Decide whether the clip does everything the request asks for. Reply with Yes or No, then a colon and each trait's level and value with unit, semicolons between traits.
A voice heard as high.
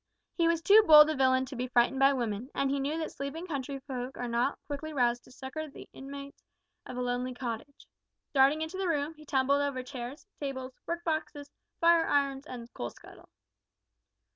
Yes: very high, 275 Hz